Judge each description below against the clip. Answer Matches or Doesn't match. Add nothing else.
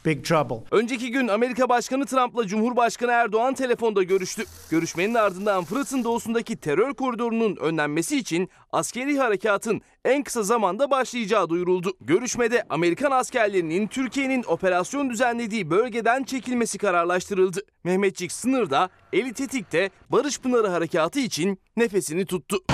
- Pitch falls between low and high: Doesn't match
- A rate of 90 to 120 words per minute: Matches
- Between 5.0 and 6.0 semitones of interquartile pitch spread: Matches